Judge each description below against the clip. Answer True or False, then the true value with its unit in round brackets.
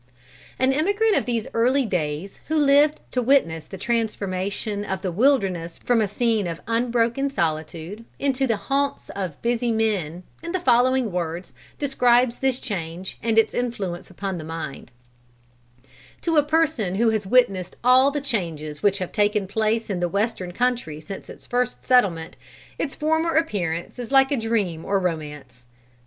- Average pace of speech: True (160 wpm)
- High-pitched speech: True (220 Hz)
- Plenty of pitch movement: True (6.0 semitones)